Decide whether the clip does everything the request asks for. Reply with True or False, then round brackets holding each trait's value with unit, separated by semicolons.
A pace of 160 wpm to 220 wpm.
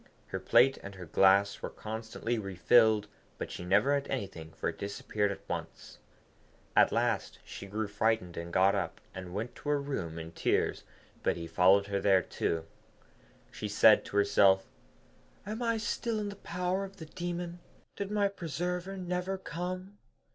True (165 wpm)